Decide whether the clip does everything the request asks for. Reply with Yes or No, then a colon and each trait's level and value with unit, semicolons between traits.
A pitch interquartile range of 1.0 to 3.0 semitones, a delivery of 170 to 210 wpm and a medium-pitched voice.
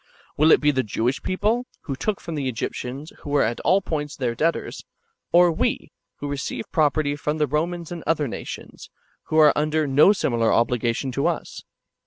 No: average, 3.4 semitones; average, 185 wpm; medium, 150 Hz